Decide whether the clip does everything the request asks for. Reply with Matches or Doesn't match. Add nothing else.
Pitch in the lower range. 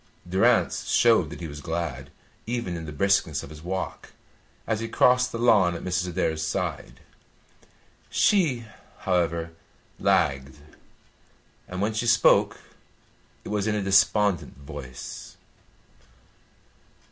Matches